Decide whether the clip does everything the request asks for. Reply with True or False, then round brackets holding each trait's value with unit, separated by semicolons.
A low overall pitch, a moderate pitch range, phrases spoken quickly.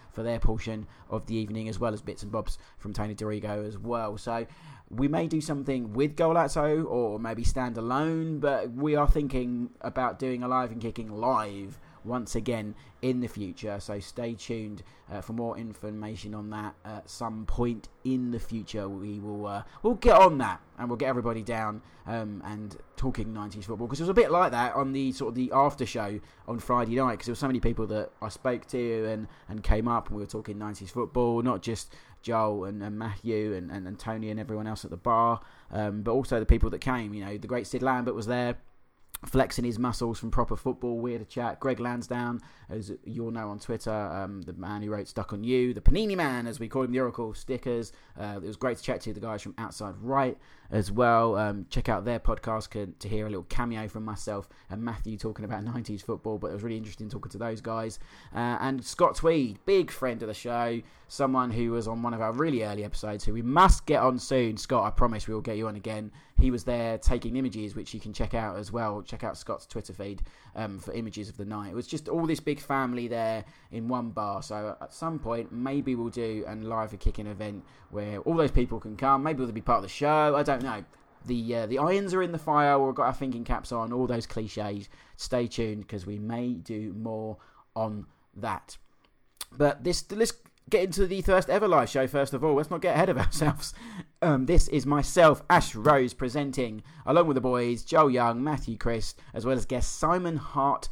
True (115 Hz; 3.3 semitones; 225 wpm)